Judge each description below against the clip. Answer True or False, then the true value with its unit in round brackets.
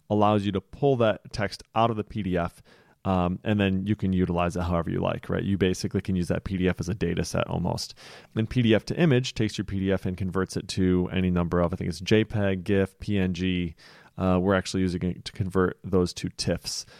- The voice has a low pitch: True (95 Hz)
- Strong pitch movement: False (2.5 semitones)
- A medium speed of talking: False (220 wpm)